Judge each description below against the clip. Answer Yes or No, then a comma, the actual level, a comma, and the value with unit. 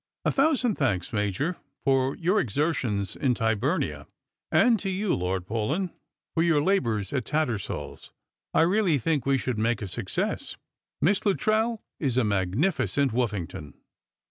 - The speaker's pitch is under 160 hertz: Yes, low, 135 Hz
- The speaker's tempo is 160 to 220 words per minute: No, average, 140 wpm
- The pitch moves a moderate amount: No, wide, 9.0 semitones